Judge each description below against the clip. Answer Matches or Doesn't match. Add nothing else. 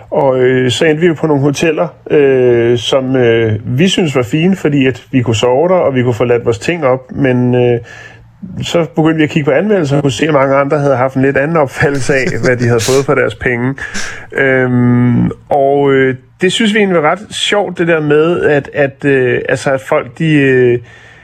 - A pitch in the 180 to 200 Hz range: Doesn't match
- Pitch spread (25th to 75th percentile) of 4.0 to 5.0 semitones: Doesn't match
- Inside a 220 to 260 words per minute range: Matches